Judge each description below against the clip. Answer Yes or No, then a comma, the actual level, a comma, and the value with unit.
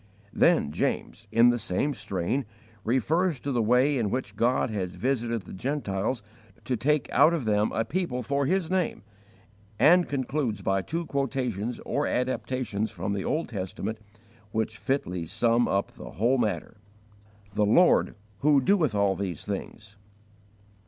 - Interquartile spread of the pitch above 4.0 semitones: Yes, average, 5.2 semitones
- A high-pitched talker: No, low, 120 Hz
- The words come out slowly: No, average, 150 wpm